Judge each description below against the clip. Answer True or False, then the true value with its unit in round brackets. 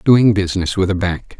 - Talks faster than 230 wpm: False (215 wpm)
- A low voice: True (95 Hz)